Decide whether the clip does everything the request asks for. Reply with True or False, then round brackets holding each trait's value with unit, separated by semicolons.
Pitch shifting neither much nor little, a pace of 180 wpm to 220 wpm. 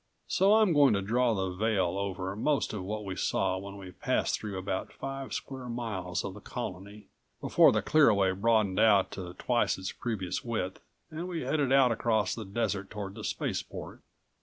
True (4.3 semitones; 185 wpm)